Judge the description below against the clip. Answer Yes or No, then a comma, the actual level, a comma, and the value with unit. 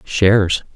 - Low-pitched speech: Yes, very low, 95 Hz